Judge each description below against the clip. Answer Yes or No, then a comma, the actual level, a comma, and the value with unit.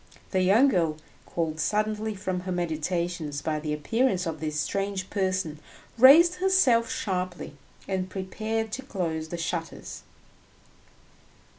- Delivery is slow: Yes, slow, 125 wpm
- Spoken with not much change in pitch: No, average, 4.9 semitones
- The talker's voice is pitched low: No, medium, 185 Hz